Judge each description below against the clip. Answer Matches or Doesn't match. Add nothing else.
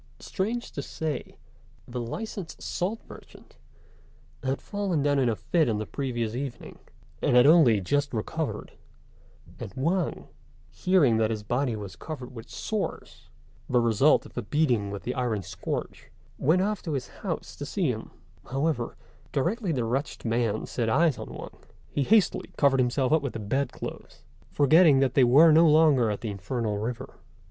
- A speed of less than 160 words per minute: Doesn't match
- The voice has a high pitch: Doesn't match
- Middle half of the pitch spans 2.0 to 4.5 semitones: Doesn't match